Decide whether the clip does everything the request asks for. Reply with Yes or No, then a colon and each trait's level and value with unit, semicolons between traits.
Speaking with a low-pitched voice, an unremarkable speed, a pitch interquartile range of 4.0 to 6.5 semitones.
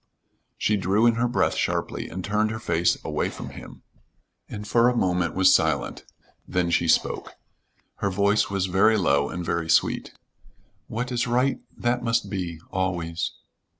Yes: low, 100 Hz; average, 160 wpm; average, 4.5 semitones